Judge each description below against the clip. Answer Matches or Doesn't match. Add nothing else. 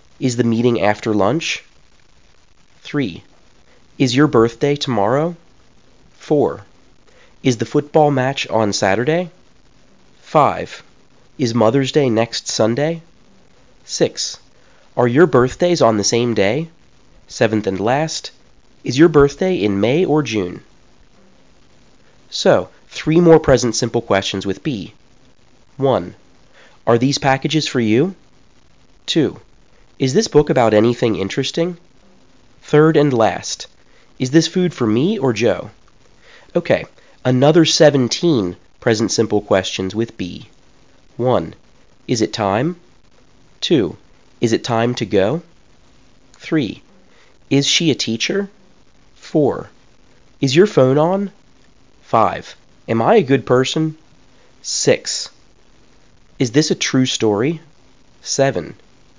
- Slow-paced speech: Matches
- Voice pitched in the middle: Doesn't match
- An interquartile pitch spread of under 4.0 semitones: Doesn't match